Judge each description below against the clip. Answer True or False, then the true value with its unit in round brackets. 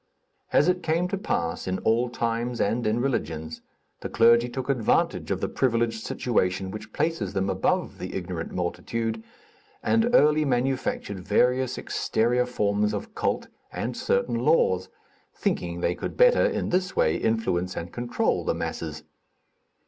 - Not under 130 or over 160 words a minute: True (150 wpm)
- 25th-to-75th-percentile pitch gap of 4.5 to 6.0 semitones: True (5.6 semitones)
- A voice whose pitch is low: True (115 Hz)